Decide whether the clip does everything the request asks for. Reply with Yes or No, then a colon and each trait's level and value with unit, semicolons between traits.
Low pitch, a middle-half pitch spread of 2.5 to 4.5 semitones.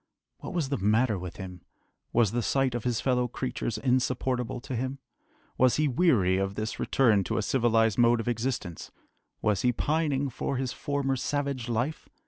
Yes: low, 125 Hz; average, 3.2 semitones